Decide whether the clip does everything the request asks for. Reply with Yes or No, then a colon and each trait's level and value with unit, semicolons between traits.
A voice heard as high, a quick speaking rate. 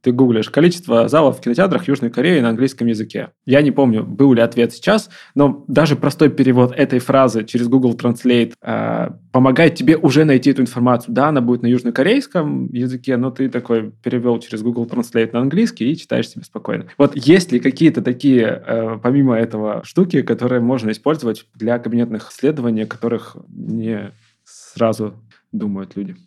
No: low, 125 Hz; fast, 170 wpm